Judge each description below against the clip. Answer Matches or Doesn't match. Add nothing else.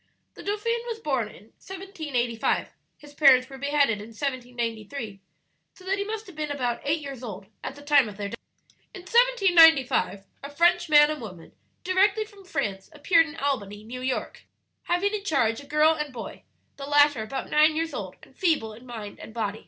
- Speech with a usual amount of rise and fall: Doesn't match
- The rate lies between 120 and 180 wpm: Doesn't match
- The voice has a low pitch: Doesn't match